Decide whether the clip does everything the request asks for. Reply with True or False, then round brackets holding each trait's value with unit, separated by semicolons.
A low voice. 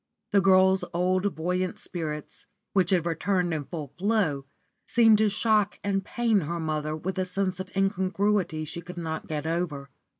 False (180 Hz)